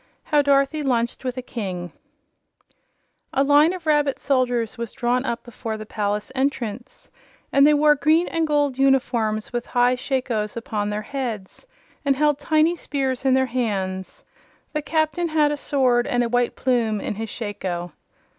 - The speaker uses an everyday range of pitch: Yes, average, 4.4 semitones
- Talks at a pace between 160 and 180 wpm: Yes, average, 165 wpm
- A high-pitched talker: Yes, very high, 255 Hz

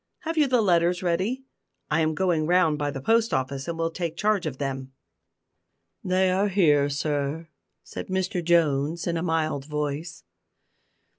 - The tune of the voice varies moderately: Yes, average, 4.0 semitones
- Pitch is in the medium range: Yes, medium, 165 Hz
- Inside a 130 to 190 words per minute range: Yes, average, 160 wpm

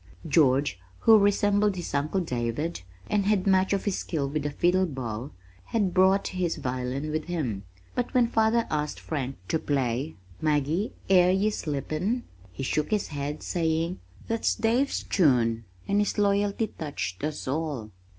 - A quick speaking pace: No, average, 155 wpm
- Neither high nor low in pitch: Yes, medium, 160 Hz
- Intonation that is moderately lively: No, wide, 6.2 semitones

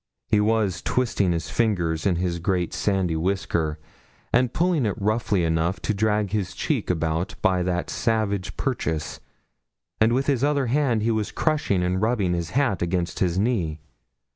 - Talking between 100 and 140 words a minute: No, average, 165 wpm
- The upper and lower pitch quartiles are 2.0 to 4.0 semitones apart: No, average, 4.5 semitones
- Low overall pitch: Yes, low, 100 Hz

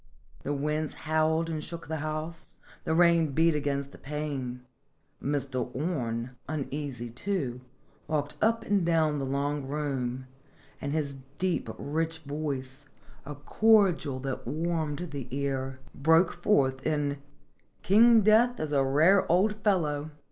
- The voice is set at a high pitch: No, medium, 150 Hz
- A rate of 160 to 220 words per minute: No, slow, 135 wpm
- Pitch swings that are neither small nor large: Yes, average, 3.2 semitones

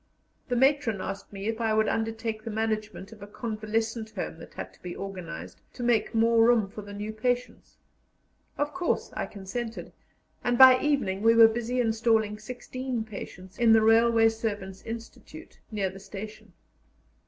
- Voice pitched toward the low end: No, high, 225 Hz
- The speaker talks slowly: No, average, 165 wpm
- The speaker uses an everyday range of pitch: No, narrow, 2.0 semitones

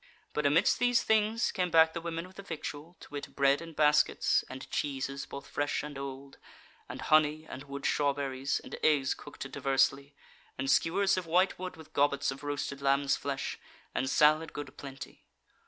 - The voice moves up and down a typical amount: Yes, average, 3.0 semitones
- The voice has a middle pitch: Yes, medium, 145 Hz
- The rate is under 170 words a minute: No, average, 175 wpm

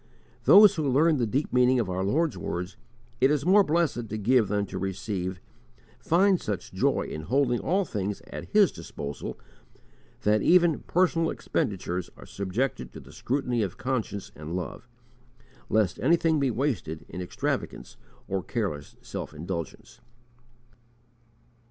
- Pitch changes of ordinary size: No, wide, 8.0 semitones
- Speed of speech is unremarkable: Yes, average, 145 wpm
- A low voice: Yes, low, 115 Hz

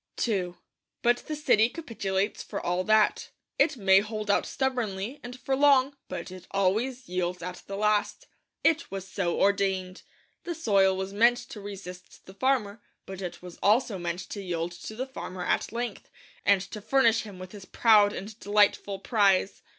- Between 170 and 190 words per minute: Yes, average, 175 wpm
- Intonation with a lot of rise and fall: No, average, 3.8 semitones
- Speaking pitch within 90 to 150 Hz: No, high, 205 Hz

